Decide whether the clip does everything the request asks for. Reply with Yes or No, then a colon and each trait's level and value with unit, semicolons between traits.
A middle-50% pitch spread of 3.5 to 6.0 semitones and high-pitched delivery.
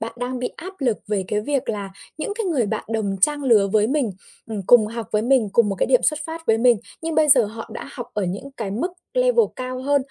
Yes: average, 5.2 semitones; high, 245 Hz